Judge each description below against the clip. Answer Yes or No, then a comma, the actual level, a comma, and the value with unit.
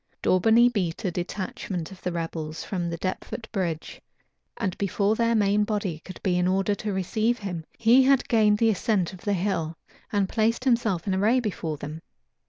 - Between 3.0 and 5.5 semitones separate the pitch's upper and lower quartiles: Yes, average, 3.7 semitones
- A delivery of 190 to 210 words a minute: No, average, 180 wpm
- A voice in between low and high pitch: No, high, 195 Hz